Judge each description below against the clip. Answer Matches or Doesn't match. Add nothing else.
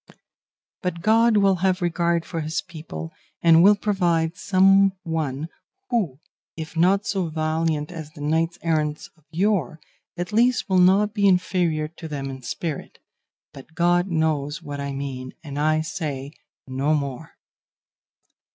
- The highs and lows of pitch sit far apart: Doesn't match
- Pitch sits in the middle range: Matches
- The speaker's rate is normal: Matches